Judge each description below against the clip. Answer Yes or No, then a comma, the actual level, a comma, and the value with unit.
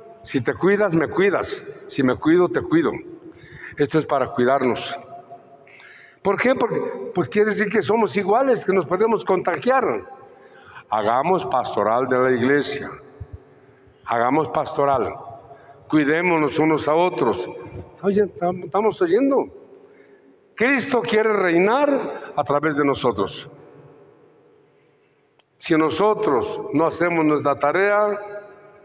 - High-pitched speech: Yes, high, 200 Hz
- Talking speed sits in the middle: No, slow, 115 wpm